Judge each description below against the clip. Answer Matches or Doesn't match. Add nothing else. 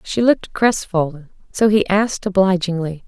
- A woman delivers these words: Matches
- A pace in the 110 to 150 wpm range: Matches